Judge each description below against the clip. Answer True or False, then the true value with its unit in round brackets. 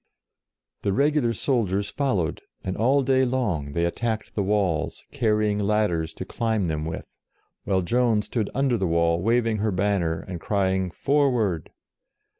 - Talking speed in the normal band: True (150 wpm)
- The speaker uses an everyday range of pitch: True (4.6 semitones)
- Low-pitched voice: True (105 Hz)